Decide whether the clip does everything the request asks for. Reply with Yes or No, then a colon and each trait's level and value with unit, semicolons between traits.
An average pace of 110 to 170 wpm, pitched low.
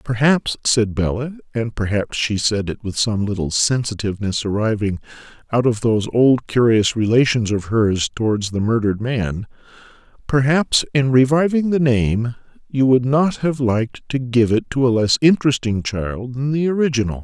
Yes: average, 160 wpm; low, 120 Hz